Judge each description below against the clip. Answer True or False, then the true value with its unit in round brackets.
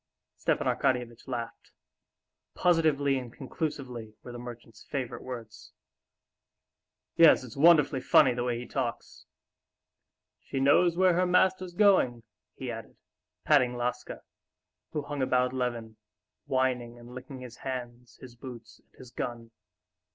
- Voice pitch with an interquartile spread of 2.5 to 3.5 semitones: True (2.9 semitones)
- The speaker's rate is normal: False (130 wpm)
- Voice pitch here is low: True (125 Hz)